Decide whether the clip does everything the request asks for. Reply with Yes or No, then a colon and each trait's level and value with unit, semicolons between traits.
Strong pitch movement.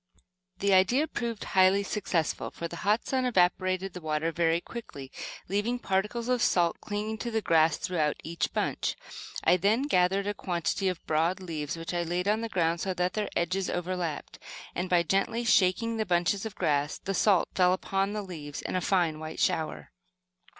No: average, 3.5 semitones